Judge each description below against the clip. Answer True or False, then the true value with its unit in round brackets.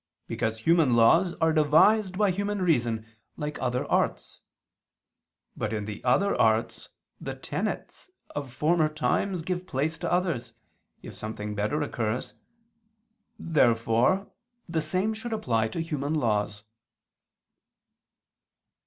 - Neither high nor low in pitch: True (150 Hz)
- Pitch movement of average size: False (7.6 semitones)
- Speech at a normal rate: False (120 wpm)